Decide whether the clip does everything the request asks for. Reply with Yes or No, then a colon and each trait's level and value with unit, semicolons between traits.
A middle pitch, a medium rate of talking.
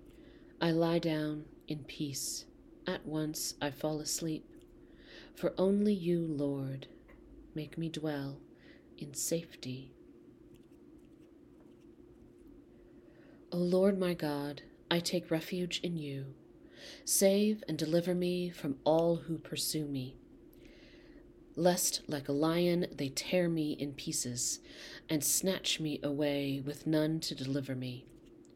No: medium, 165 Hz; slow, 115 wpm